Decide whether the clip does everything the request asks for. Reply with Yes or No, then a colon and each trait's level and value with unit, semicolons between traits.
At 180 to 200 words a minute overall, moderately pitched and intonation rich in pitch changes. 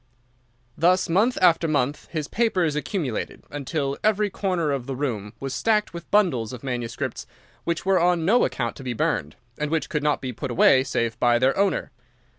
Yes: average, 185 wpm; medium, 150 Hz; wide, 6.1 semitones